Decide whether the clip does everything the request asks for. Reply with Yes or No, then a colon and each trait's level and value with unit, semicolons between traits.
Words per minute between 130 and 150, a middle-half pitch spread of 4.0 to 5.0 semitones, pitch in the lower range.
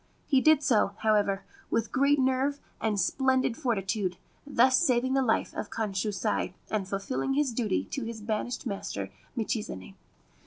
No: average, 145 wpm; average, 4.3 semitones; high, 230 Hz